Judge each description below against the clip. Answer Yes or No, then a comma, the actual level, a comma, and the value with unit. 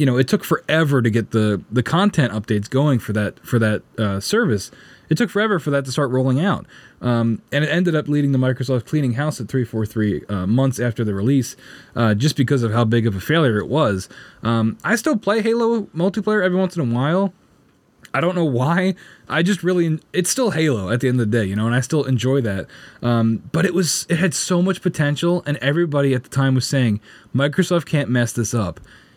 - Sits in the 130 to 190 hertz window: Yes, low, 135 Hz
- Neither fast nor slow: No, fast, 230 wpm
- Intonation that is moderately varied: No, wide, 6.5 semitones